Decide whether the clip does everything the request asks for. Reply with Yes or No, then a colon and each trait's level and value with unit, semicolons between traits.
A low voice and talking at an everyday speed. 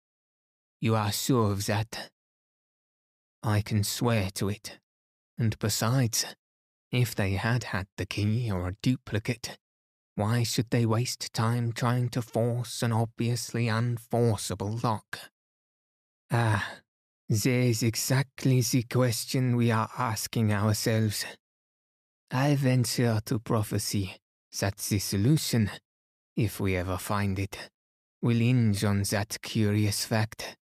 No: low, 110 Hz; slow, 120 wpm